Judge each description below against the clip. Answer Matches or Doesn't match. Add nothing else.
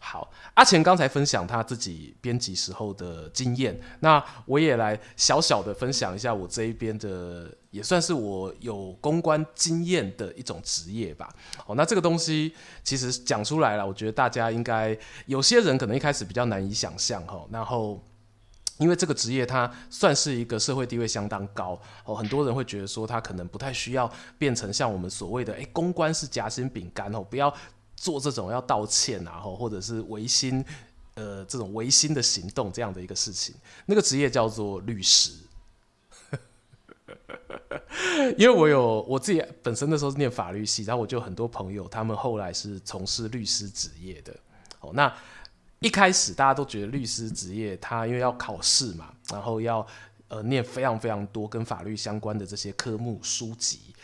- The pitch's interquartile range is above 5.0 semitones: Doesn't match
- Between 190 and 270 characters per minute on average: Doesn't match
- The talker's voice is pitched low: Matches